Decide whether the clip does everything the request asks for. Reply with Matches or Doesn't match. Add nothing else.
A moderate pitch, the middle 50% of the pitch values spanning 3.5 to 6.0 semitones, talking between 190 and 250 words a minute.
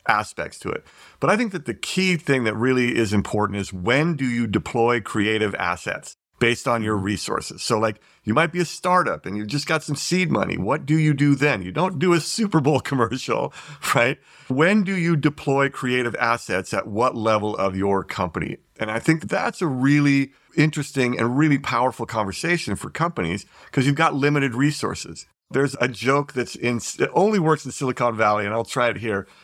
Doesn't match